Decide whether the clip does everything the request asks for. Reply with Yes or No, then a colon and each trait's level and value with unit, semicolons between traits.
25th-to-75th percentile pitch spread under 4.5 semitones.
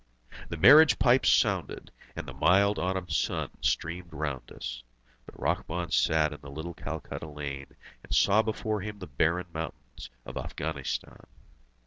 No: average, 4.8 semitones